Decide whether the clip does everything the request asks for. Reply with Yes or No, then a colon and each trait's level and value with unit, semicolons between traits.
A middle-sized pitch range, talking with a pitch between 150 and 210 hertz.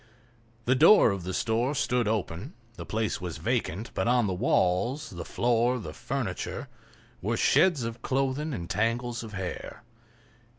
No: average, 4.6 semitones; low, 115 Hz